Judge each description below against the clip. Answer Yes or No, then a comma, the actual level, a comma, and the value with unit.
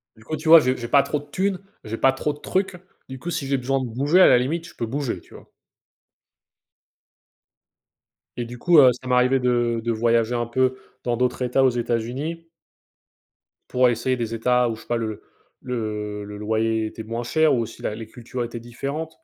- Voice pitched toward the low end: Yes, low, 125 Hz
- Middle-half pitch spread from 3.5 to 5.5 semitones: No, average, 3.0 semitones